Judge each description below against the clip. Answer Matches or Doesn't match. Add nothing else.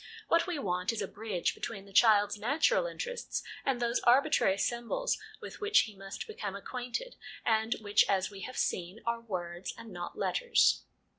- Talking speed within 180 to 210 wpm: Doesn't match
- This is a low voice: Doesn't match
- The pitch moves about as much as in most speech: Doesn't match